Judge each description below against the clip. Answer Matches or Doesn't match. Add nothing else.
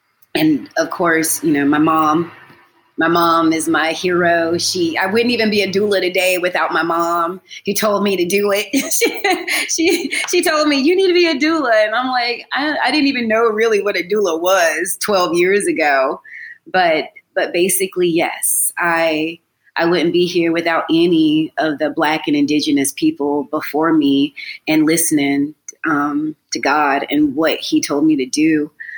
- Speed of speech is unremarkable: Matches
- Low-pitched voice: Doesn't match